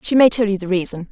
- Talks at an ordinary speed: No, fast, 325 wpm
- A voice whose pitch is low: No, high, 205 Hz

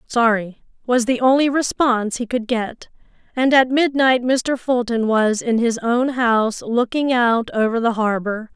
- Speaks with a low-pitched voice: No, high, 240 Hz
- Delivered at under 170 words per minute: Yes, average, 160 wpm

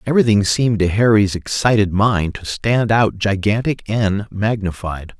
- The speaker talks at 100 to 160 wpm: Yes, average, 140 wpm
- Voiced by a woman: No, male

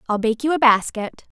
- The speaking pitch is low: No, high, 240 Hz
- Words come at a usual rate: No, fast, 215 wpm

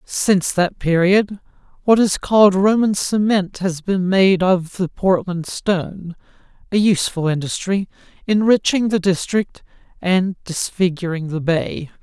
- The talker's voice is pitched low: No, medium, 185 Hz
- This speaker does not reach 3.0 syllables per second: No, 4.2 syllables/s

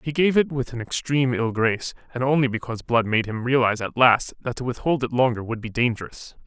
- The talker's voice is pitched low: Yes, low, 125 Hz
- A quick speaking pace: Yes, fast, 230 wpm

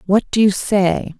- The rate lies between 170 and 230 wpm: Yes, average, 200 wpm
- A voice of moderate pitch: No, high, 195 Hz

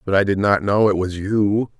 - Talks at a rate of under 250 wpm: No, fast, 270 wpm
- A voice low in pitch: Yes, low, 100 Hz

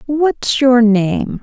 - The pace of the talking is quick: No, slow, 125 wpm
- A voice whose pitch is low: No, very high, 250 Hz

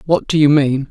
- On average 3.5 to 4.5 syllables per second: No, 5.2 syllables/s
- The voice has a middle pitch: Yes, medium, 145 Hz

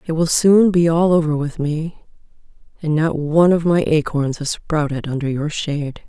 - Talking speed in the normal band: Yes, average, 190 wpm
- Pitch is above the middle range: No, medium, 160 Hz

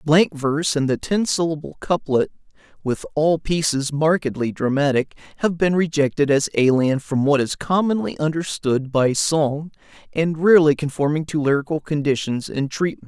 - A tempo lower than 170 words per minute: Yes, average, 145 wpm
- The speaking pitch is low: No, medium, 150 Hz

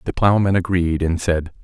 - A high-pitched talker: No, very low, 85 Hz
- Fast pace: No, average, 185 wpm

